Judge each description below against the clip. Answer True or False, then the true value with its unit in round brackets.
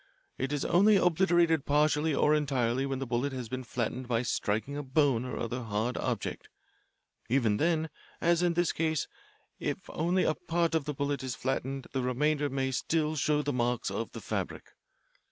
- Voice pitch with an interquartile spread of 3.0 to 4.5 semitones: True (3.9 semitones)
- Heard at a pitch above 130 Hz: True (140 Hz)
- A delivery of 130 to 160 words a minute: False (180 wpm)